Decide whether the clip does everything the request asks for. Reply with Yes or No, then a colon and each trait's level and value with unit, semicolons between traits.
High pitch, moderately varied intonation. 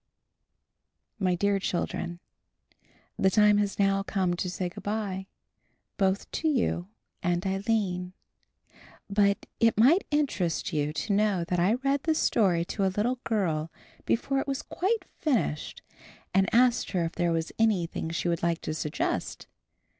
Yes: high, 195 Hz; average, 4.2 semitones